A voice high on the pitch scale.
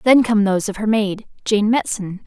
Yes: high, 210 Hz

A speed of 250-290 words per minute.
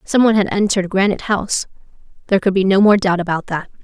No: fast, 205 wpm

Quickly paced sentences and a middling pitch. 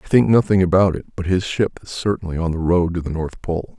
No: fast, 270 wpm; very low, 90 Hz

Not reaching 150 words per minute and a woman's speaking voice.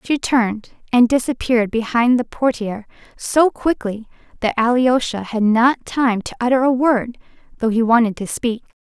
No: average, 155 wpm; female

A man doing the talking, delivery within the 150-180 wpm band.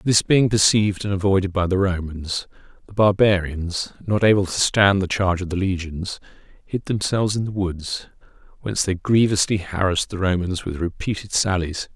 Yes: male; average, 165 wpm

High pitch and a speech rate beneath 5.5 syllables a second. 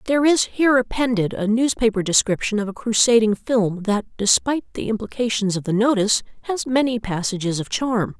No: high, 225 Hz; 5.6 syllables/s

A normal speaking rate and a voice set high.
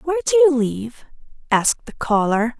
Yes: average, 160 wpm; very high, 270 Hz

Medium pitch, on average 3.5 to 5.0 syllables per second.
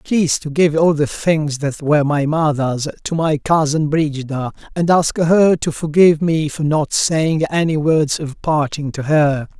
Yes: medium, 155 Hz; 4.4 syllables/s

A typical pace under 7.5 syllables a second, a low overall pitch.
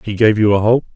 Yes: 6.4 syllables/s; low, 110 Hz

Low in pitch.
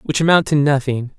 No: medium, 145 Hz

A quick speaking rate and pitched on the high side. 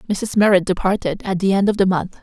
Yes: fast, 245 wpm; high, 195 Hz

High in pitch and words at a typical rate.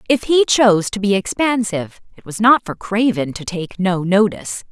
Yes: high, 205 Hz; average, 190 wpm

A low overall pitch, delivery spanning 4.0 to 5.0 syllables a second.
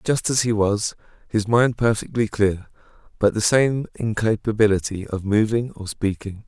Yes: low, 105 Hz; 4.6 syllables/s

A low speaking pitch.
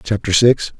Yes: low, 105 Hz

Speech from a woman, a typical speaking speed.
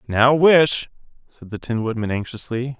No: male; average, 150 wpm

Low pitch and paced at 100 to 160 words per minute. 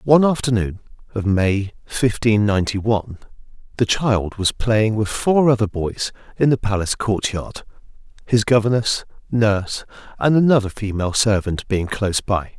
Yes: low, 110 Hz; average, 140 wpm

